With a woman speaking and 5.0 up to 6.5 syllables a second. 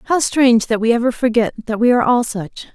Yes: female; 5.7 syllables/s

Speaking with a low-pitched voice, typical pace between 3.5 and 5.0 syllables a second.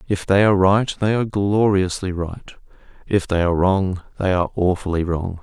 No: very low, 95 Hz; 5.5 syllables/s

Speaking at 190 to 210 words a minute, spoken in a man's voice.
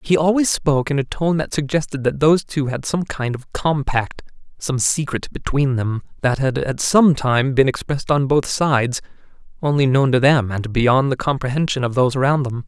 Yes: average, 200 wpm; male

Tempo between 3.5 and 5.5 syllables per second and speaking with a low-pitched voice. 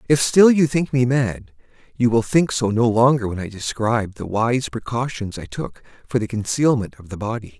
Yes: 5.0 syllables/s; low, 120 Hz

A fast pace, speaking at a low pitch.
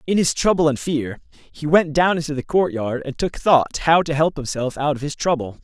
No: fast, 235 wpm; medium, 150 Hz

